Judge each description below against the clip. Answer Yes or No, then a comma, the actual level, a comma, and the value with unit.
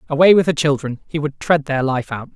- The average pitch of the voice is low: No, medium, 145 Hz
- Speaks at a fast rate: Yes, fast, 255 wpm